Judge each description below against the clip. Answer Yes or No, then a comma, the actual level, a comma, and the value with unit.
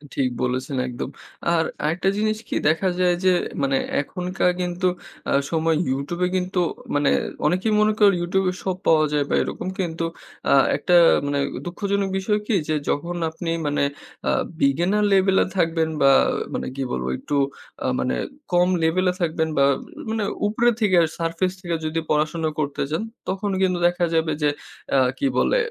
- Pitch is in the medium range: Yes, medium, 175 Hz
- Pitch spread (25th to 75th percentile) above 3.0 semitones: Yes, average, 3.7 semitones